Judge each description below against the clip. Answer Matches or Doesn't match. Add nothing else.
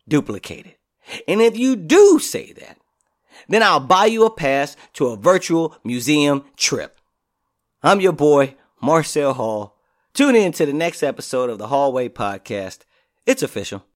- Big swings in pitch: Matches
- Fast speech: Doesn't match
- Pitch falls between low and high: Matches